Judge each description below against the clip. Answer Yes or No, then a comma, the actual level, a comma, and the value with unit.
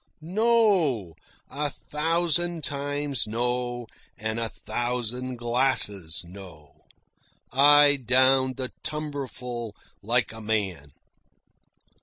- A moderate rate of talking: No, slow, 85 wpm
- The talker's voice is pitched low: Yes, low, 125 Hz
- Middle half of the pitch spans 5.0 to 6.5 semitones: No, average, 4.5 semitones